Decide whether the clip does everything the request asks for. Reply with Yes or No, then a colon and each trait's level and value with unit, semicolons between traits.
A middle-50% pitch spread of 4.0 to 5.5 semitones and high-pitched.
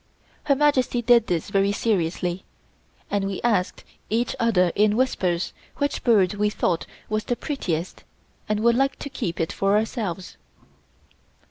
Yes: average, 4.5 semitones; high, 210 Hz